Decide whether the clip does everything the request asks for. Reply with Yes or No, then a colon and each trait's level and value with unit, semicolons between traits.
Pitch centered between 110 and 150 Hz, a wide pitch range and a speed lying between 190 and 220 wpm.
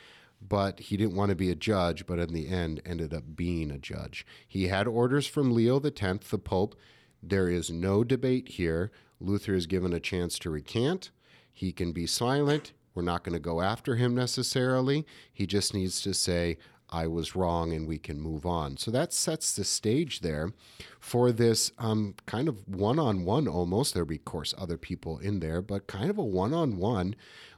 No: low, 100 Hz; wide, 6.0 semitones; average, 200 wpm